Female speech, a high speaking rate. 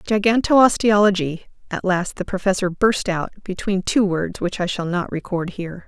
No: female; average, 165 wpm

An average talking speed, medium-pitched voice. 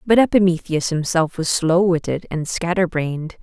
Yes: average, 160 wpm; medium, 170 Hz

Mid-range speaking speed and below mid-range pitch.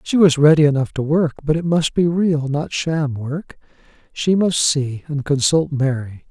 No: average, 190 wpm; medium, 150 Hz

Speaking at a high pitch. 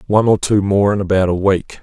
No: low, 100 Hz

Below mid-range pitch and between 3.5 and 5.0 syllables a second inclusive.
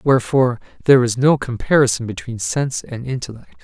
No: low, 125 Hz; 6.2 syllables/s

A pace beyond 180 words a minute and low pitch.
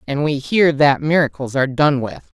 No: average, 200 wpm; medium, 145 Hz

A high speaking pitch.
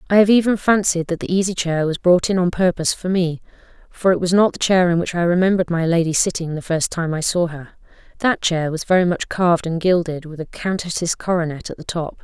No: medium, 175 Hz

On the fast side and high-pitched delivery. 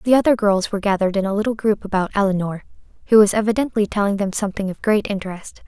Yes: fast, 210 wpm; high, 205 Hz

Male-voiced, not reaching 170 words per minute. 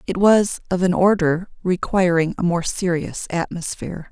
No: female; average, 145 wpm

